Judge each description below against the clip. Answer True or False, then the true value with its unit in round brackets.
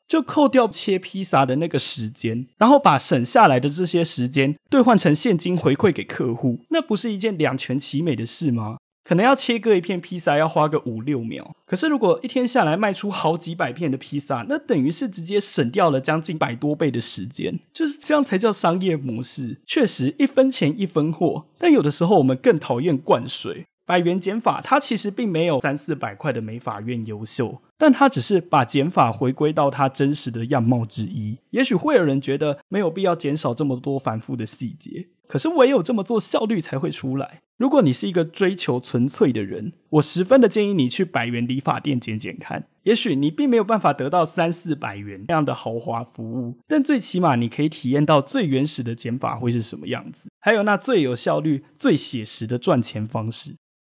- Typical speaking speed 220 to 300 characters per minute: False (315 characters per minute)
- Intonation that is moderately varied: False (7.7 semitones)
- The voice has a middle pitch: True (155 Hz)